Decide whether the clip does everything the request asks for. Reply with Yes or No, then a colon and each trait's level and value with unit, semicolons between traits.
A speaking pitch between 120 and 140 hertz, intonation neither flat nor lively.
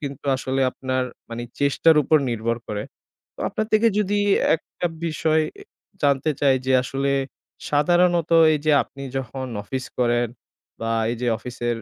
Yes: low, 135 Hz; average, 4.1 semitones